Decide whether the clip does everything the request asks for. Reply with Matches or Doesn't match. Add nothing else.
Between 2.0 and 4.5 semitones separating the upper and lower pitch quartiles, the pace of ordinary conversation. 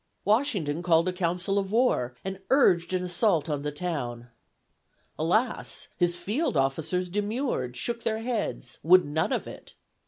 Doesn't match